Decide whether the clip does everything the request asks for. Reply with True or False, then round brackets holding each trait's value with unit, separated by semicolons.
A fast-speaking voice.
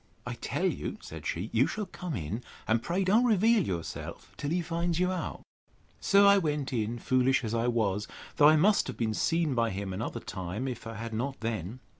True (210 wpm)